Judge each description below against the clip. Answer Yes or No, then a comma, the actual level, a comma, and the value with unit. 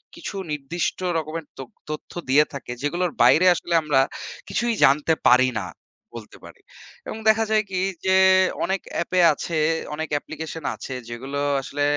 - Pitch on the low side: No, medium, 155 Hz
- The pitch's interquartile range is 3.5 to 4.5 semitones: Yes, average, 4.1 semitones